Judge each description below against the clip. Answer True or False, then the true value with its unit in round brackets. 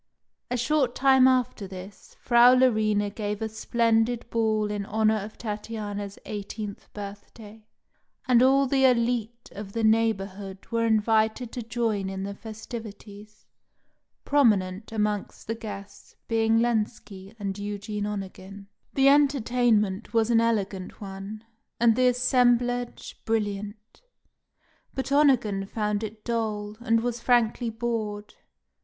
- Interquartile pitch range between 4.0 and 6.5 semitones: False (2.6 semitones)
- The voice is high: True (220 Hz)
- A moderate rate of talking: False (125 wpm)